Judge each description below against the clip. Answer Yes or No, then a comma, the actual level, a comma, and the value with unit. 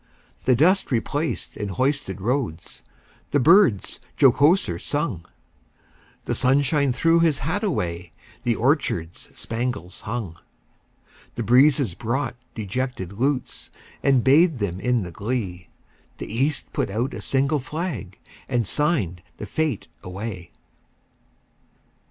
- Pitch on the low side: Yes, low, 125 Hz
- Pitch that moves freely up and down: Yes, wide, 6.4 semitones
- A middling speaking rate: No, slow, 115 wpm